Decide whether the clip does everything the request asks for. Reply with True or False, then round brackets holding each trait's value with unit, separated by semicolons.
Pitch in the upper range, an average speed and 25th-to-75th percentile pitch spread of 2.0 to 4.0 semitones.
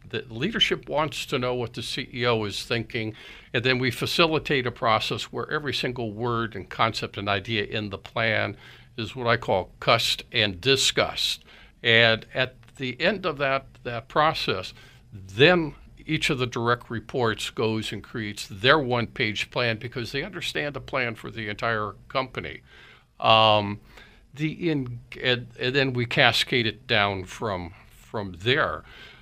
False (120 Hz; 155 wpm; 2.7 semitones)